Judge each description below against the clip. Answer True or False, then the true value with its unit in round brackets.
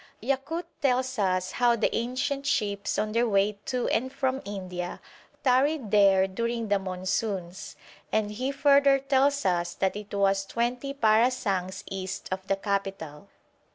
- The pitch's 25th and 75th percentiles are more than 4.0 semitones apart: True (5.0 semitones)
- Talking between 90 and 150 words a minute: True (145 wpm)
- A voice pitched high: True (215 Hz)